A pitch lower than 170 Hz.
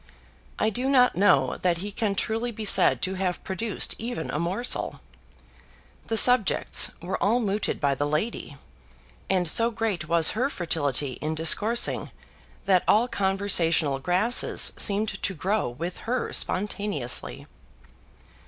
No: high, 195 Hz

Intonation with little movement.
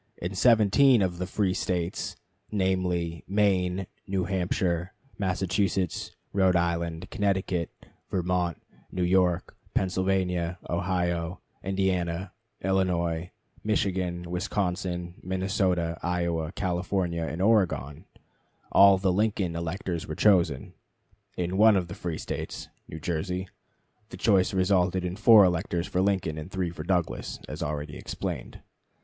Yes: narrow, 1.8 semitones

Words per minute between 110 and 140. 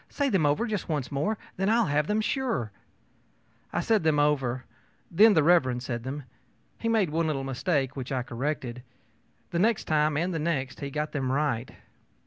No: average, 185 wpm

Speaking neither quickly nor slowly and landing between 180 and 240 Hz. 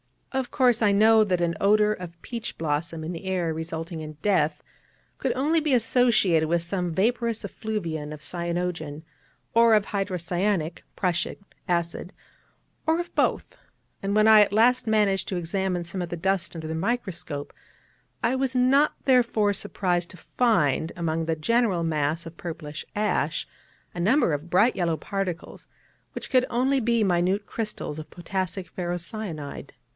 Yes: average, 155 wpm; medium, 185 Hz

